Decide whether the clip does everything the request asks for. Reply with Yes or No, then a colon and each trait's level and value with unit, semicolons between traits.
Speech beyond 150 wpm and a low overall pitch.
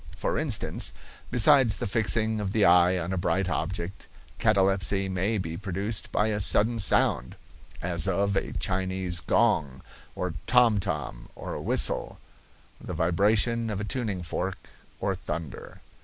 No: average, 145 wpm; very low, 95 Hz